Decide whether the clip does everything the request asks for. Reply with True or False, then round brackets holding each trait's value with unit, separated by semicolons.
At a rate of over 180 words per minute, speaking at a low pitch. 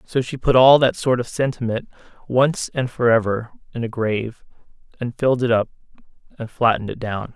True (190 wpm; 120 Hz)